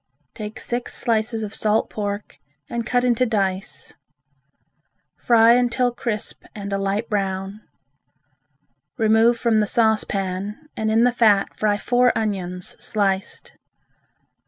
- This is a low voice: No, high, 215 Hz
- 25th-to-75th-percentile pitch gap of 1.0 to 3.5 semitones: Yes, average, 2.7 semitones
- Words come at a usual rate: No, slow, 120 wpm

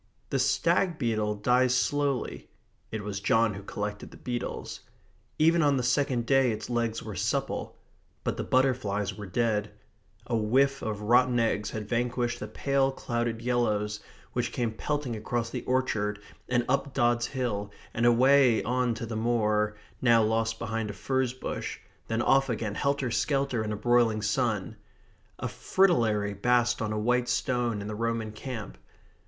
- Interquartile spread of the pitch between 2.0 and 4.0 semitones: Yes, average, 3.0 semitones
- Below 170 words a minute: Yes, average, 160 wpm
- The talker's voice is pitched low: Yes, low, 120 Hz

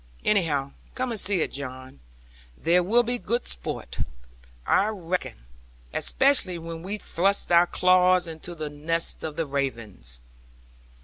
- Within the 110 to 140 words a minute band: Yes, slow, 135 wpm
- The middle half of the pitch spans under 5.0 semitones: No, average, 5.3 semitones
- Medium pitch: Yes, medium, 170 Hz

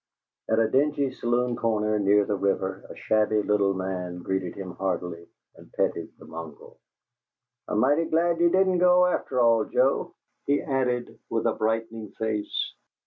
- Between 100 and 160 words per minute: Yes, average, 155 wpm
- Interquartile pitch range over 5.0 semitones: Yes, wide, 5.4 semitones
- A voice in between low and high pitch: No, low, 110 Hz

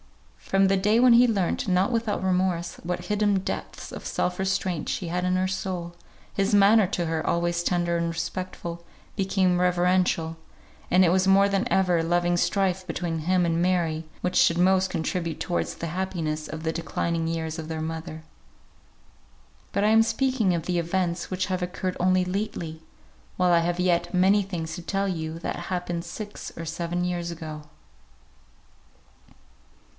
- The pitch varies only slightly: Yes, narrow, 2.0 semitones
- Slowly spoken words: No, average, 170 wpm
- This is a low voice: No, medium, 180 Hz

